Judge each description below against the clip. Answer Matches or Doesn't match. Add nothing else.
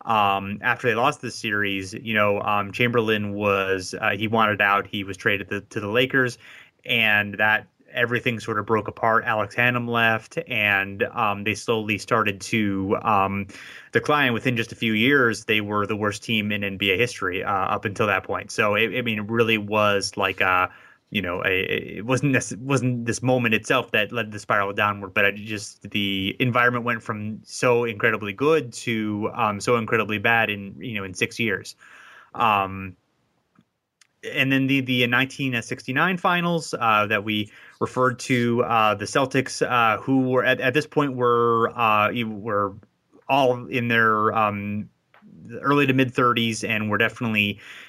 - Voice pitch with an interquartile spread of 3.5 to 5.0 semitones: Doesn't match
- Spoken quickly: Doesn't match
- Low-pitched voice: Matches